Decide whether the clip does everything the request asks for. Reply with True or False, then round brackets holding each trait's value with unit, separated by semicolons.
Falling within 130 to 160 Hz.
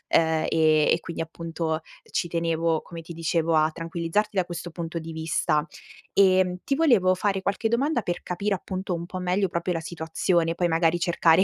False (170 Hz)